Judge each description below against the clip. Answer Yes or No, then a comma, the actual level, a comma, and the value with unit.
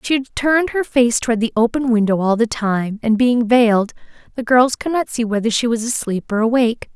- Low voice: No, high, 235 Hz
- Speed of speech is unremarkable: No, fast, 225 wpm